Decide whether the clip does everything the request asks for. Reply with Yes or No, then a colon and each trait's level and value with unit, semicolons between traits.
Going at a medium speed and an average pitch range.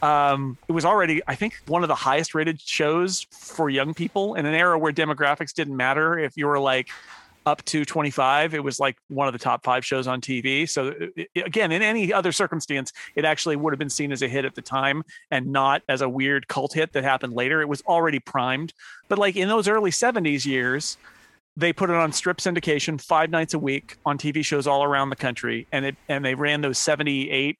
No: fast, 230 wpm; average, 3.1 semitones